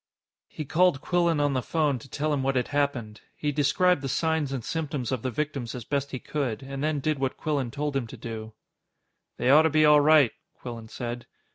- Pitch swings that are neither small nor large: Yes, average, 3.2 semitones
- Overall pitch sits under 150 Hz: Yes, medium, 140 Hz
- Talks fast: Yes, fast, 220 wpm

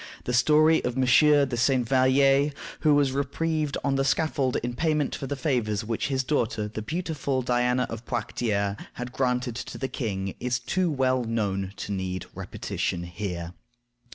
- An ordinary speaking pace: Yes, average, 165 wpm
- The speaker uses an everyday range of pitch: Yes, average, 3.9 semitones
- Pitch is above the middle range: No, low, 125 Hz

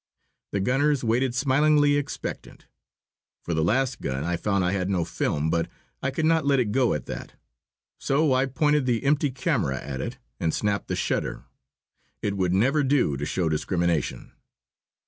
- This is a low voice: Yes, low, 120 Hz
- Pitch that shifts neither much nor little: No, wide, 7.9 semitones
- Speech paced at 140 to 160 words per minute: No, average, 170 wpm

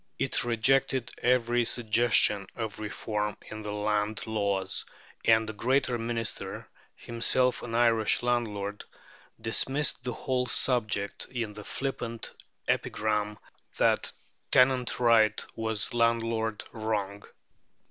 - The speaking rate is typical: No, slow, 105 wpm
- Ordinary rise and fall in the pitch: No, narrow, 2.3 semitones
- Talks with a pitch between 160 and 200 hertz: No, low, 115 Hz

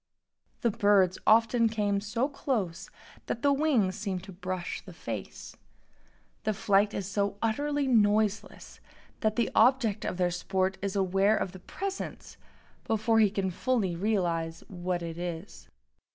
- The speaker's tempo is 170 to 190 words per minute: No, average, 145 wpm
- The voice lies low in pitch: No, high, 200 Hz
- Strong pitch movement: No, average, 3.2 semitones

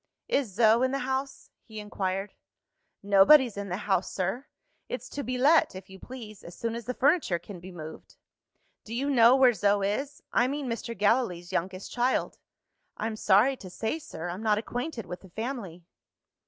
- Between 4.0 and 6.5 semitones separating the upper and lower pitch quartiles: Yes, average, 5.2 semitones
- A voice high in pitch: Yes, high, 220 Hz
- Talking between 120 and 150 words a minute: No, average, 180 wpm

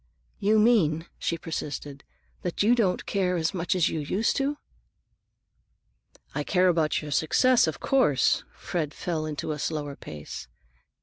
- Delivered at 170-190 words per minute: No, average, 145 wpm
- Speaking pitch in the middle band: Yes, medium, 165 Hz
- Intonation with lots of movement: No, average, 4.7 semitones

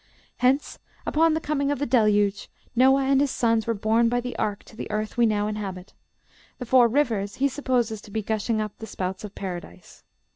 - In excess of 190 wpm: Yes, fast, 205 wpm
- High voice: Yes, high, 225 Hz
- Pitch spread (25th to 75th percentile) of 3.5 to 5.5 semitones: Yes, average, 3.8 semitones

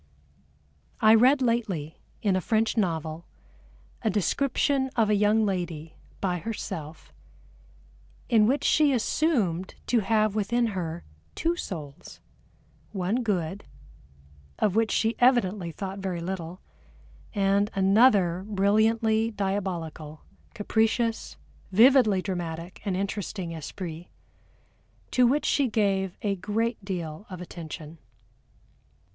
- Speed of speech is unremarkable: No, slow, 110 wpm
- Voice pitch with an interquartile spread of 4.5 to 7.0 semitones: No, average, 4.1 semitones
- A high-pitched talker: Yes, high, 200 Hz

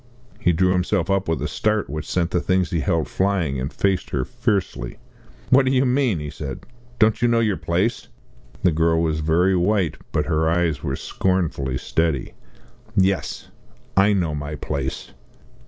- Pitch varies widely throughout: No, average, 4.0 semitones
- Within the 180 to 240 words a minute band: No, average, 170 wpm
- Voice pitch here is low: Yes, very low, 90 Hz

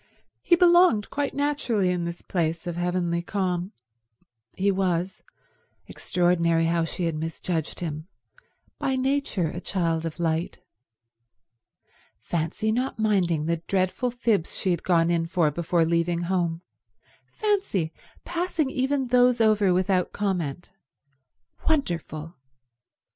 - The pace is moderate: No, slow, 115 wpm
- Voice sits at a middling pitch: Yes, medium, 180 Hz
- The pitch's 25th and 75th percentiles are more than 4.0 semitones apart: Yes, average, 4.6 semitones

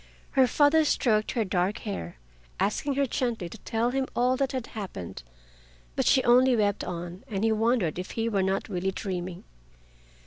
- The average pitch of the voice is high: Yes, high, 220 Hz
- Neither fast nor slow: Yes, average, 175 wpm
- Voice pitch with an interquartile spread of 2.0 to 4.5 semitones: No, average, 5.0 semitones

